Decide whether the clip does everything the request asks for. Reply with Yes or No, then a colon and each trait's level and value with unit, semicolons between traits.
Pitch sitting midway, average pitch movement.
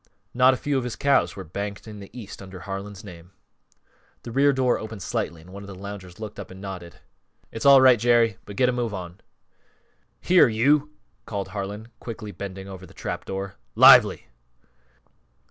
No: low, 100 Hz; average, 4.1 semitones